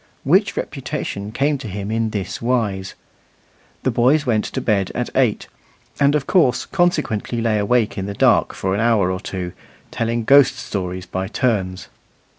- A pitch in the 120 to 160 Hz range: No, low, 110 Hz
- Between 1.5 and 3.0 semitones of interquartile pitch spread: No, average, 4.3 semitones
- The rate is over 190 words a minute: No, average, 165 wpm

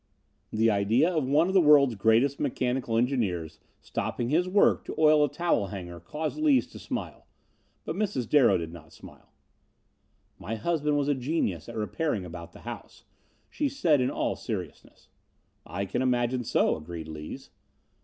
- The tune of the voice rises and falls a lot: Yes, wide, 7.3 semitones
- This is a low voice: Yes, low, 125 Hz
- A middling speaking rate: Yes, average, 165 wpm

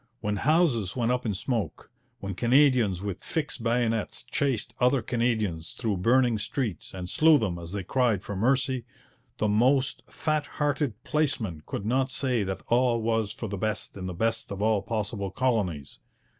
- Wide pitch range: No, average, 4.3 semitones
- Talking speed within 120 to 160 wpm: No, average, 170 wpm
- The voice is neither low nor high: No, low, 115 Hz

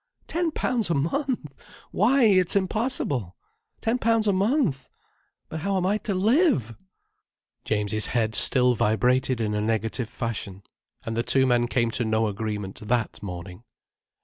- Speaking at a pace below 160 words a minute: Yes, average, 150 wpm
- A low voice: Yes, low, 125 Hz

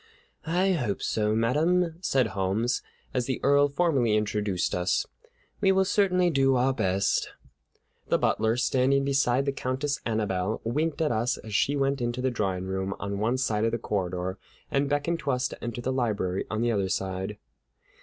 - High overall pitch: No, low, 120 Hz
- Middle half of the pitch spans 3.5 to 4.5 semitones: No, average, 4.9 semitones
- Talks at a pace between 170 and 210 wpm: Yes, average, 175 wpm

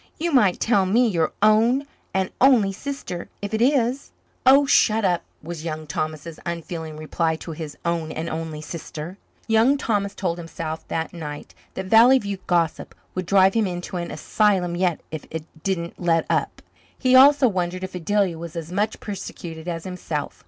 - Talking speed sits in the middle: Yes, average, 175 wpm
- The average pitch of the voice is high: No, medium, 180 Hz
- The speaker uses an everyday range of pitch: Yes, average, 4.6 semitones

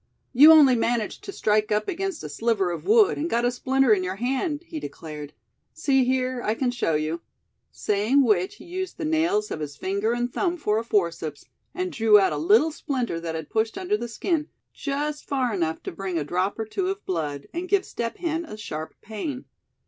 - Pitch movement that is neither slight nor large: No, wide, 8.3 semitones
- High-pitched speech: Yes, high, 235 Hz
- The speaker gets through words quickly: Yes, fast, 210 wpm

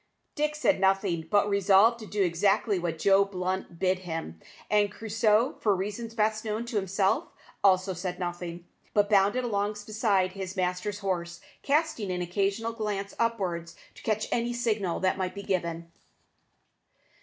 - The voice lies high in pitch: Yes, high, 195 Hz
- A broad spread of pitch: No, average, 2.8 semitones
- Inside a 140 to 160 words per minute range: Yes, average, 155 wpm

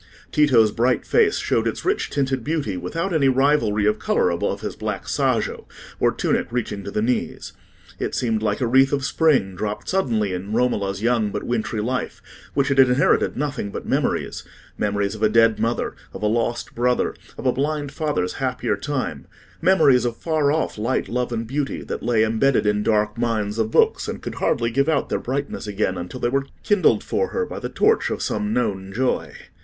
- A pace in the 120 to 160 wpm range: No, average, 190 wpm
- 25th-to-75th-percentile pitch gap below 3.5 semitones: No, average, 4.6 semitones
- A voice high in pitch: No, low, 120 Hz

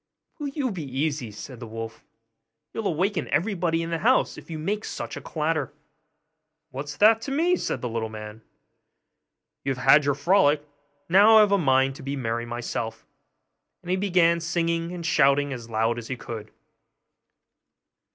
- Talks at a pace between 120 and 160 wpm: No, average, 170 wpm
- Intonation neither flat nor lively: No, wide, 6.7 semitones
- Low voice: No, medium, 150 Hz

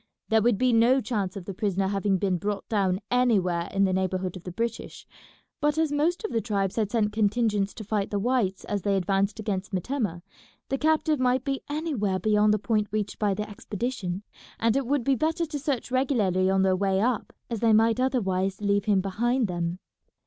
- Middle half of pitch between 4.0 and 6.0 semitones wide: Yes, average, 4.3 semitones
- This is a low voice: No, high, 210 Hz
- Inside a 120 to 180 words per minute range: No, fast, 205 wpm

